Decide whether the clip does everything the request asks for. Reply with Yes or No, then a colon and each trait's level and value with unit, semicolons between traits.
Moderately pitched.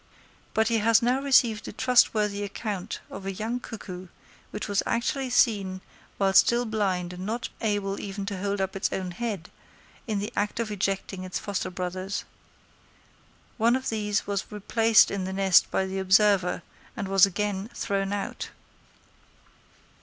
No: high, 205 Hz